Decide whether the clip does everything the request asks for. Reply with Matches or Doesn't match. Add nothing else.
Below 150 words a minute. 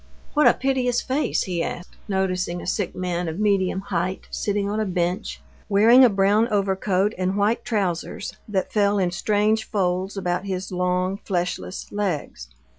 Doesn't match